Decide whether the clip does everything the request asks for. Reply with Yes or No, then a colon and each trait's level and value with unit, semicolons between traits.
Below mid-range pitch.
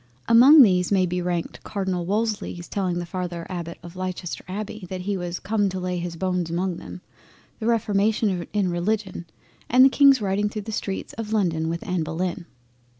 No: medium, 185 Hz